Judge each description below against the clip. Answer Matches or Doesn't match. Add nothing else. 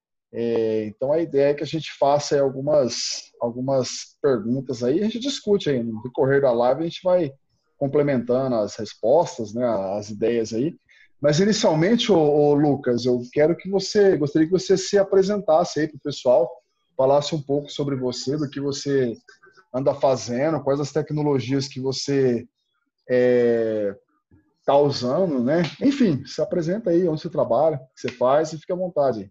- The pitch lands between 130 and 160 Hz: Matches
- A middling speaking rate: Matches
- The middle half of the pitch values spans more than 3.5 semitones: Matches